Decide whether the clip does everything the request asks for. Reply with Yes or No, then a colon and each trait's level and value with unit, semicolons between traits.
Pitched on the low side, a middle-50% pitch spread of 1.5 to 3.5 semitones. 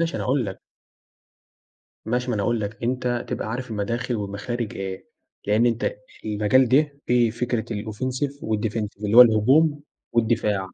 Yes: low, 115 Hz; average, 3.1 semitones